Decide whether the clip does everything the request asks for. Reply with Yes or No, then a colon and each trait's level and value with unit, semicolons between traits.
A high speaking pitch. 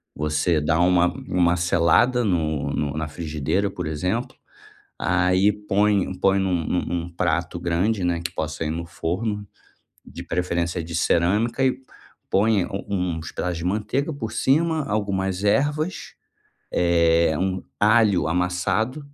No: very low, 90 Hz